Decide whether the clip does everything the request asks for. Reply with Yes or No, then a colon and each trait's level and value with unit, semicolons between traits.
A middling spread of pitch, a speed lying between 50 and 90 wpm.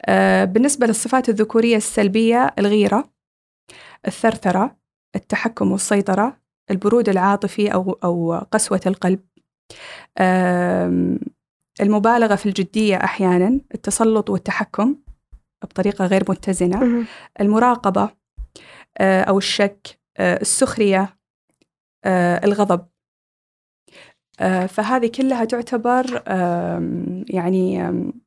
Yes: average, 3.5 semitones; average, 70 wpm